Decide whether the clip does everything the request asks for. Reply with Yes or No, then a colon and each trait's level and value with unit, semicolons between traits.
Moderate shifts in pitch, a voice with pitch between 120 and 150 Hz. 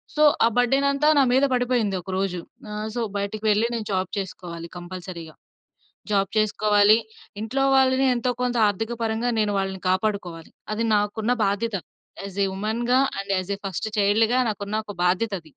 No: average, 3.2 semitones; high, 210 Hz